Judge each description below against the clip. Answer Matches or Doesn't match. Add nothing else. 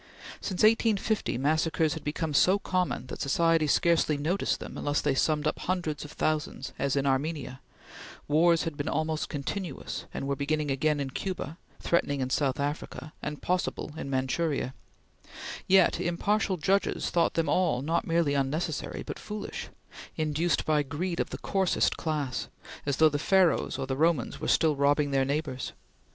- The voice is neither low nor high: Matches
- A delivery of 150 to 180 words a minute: Matches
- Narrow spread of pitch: Doesn't match